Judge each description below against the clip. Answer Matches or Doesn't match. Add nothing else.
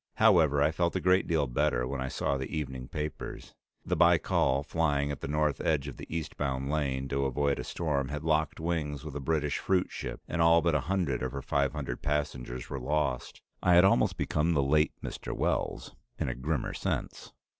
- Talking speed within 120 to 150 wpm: Doesn't match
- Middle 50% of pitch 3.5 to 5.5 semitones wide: Doesn't match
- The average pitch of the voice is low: Matches